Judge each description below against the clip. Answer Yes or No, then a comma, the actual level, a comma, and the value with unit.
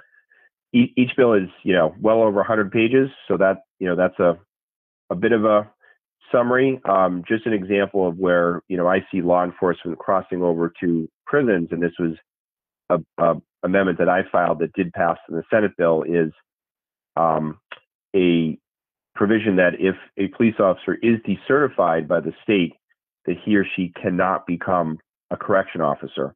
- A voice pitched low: Yes, very low, 95 Hz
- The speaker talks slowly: No, average, 170 wpm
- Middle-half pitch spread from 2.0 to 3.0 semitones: No, average, 4.0 semitones